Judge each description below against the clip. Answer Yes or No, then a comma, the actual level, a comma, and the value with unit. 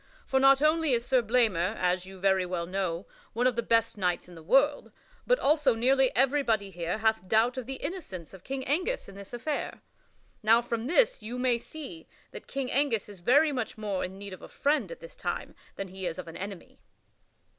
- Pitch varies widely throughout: Yes, wide, 6.0 semitones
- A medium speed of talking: No, fast, 210 wpm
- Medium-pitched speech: No, high, 230 Hz